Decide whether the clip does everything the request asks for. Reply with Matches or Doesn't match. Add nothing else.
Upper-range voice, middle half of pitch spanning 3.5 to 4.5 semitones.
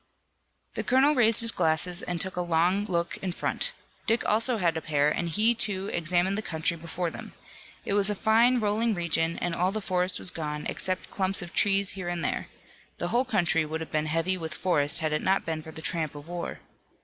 Doesn't match